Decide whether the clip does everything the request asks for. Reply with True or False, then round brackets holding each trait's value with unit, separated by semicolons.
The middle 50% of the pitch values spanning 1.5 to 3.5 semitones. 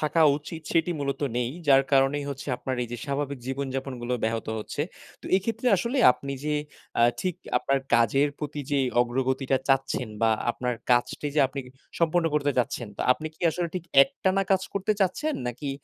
False (4.4 semitones)